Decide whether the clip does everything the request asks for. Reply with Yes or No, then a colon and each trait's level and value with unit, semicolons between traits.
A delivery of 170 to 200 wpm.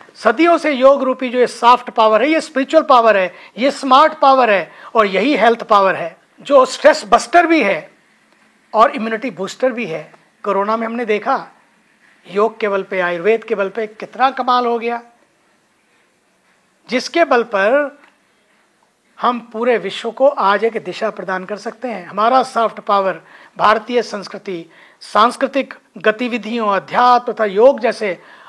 No: average, 155 wpm